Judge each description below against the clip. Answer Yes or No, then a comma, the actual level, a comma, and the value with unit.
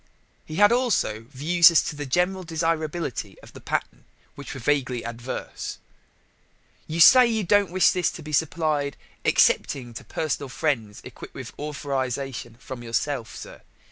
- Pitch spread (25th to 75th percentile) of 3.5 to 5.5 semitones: Yes, average, 4.9 semitones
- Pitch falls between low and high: Yes, medium, 145 Hz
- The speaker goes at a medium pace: Yes, average, 155 wpm